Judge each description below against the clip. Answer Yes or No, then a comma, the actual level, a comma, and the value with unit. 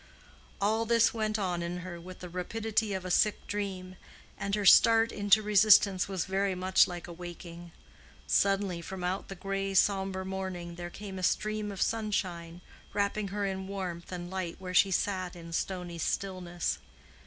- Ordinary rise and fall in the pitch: No, narrow, 2.2 semitones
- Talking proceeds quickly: No, average, 170 wpm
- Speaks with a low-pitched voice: No, high, 190 Hz